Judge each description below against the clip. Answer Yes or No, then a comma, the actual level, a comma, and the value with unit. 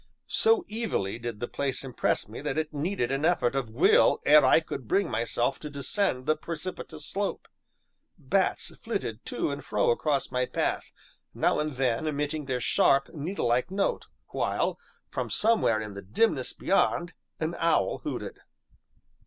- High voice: No, medium, 145 Hz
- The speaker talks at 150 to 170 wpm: Yes, average, 155 wpm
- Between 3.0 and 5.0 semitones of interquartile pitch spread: No, wide, 5.4 semitones